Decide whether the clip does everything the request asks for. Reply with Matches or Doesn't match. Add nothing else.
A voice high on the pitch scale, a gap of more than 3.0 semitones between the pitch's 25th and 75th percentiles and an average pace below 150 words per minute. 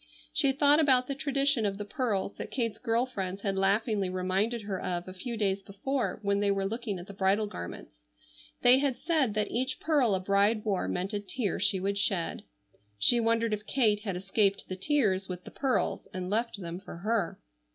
Doesn't match